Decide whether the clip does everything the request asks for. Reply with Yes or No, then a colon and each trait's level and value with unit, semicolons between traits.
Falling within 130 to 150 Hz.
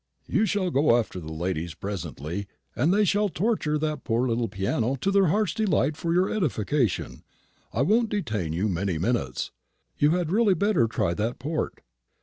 Yes: medium, 140 Hz